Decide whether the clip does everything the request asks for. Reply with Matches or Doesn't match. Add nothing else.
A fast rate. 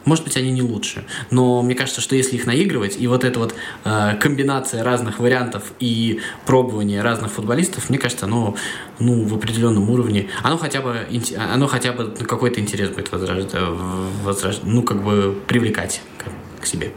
Matches